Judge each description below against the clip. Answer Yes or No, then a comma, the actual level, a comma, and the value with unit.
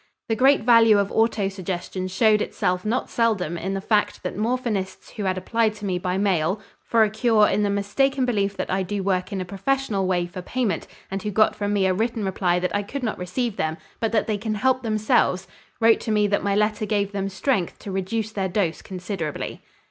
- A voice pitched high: Yes, high, 205 Hz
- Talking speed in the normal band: No, fast, 215 wpm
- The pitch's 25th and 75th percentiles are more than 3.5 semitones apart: No, average, 2.8 semitones